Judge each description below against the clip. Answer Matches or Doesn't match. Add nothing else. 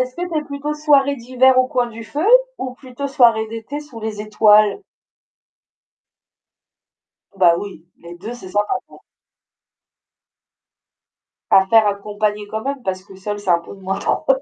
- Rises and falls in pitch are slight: Doesn't match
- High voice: Matches